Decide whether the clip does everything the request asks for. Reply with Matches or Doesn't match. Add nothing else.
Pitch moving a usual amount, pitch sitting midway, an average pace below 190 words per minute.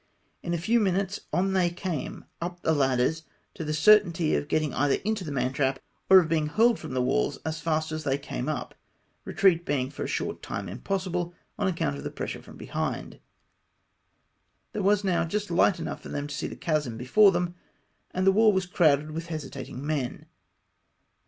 Doesn't match